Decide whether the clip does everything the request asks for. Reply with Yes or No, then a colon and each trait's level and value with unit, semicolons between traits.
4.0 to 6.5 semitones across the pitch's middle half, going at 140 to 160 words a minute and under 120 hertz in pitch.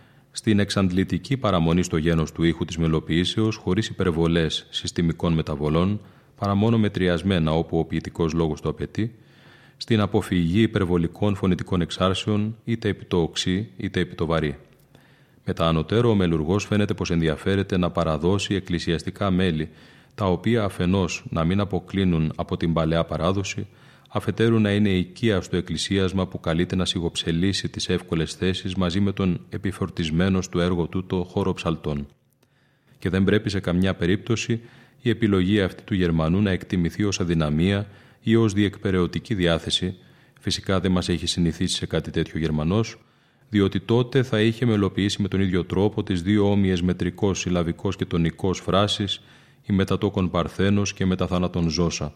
No: average, 3.5 semitones; average, 150 wpm; very low, 95 Hz